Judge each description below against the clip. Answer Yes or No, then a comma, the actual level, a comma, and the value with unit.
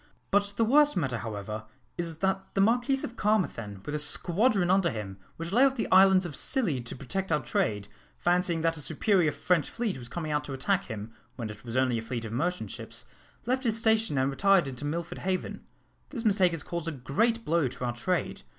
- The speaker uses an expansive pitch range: Yes, wide, 7.4 semitones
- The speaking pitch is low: No, medium, 170 Hz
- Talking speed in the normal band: No, fast, 215 wpm